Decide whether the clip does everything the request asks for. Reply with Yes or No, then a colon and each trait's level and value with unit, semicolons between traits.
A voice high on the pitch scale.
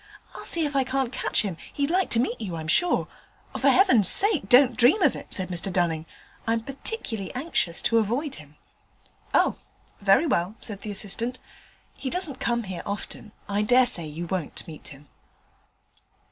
Yes: high, 225 Hz